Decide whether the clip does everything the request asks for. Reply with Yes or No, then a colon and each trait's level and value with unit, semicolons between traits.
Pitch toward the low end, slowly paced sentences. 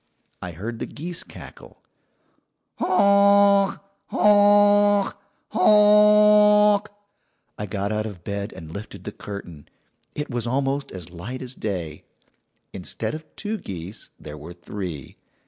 Yes: low, 130 Hz; slow, 120 wpm